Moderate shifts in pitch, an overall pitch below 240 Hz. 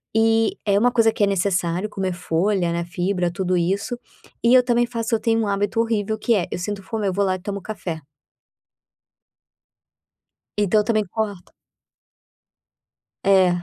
Yes: average, 3.4 semitones; high, 200 Hz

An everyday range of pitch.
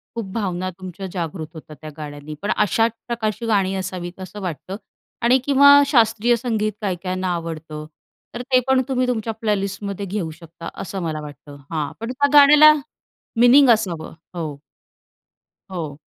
No: wide, 5.8 semitones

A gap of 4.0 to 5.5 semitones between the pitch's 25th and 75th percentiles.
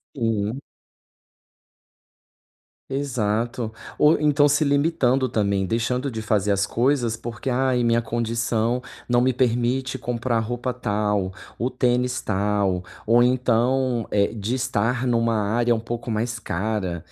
No: narrow, 2.6 semitones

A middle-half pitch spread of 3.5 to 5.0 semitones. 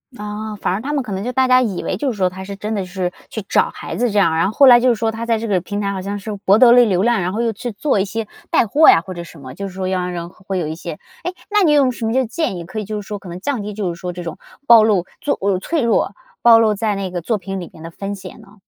Yes: average, 3.8 semitones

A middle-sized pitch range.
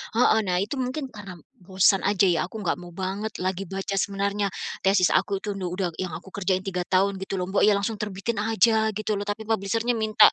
No: narrow, 2.3 semitones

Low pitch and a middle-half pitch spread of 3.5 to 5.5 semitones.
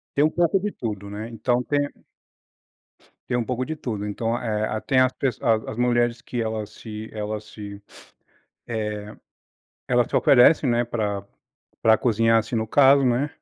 No: low, 115 Hz; average, 2.8 semitones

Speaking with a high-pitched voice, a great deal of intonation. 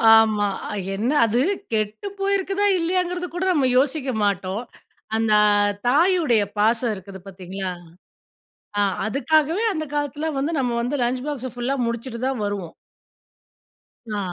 Yes: very high, 250 Hz; wide, 6.5 semitones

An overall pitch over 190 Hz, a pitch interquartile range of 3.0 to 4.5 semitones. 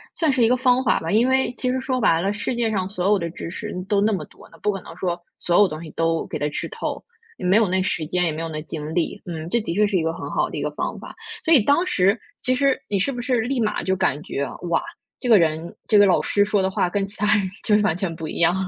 No: high, 200 Hz; average, 5.2 semitones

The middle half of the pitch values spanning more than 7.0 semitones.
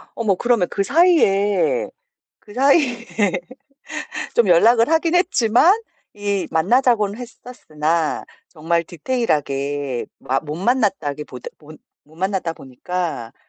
Yes: wide, 7.5 semitones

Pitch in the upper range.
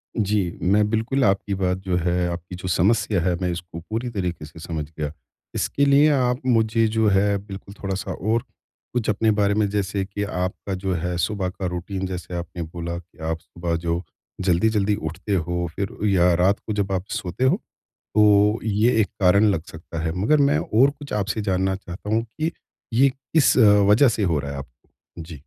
No: low, 100 Hz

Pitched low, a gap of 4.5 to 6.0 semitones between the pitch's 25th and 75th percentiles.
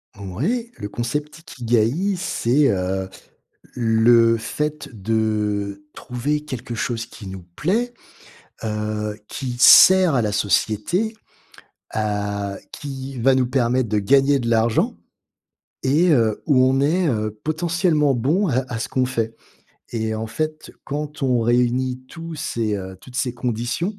Yes: low, 125 Hz; average, 5.3 semitones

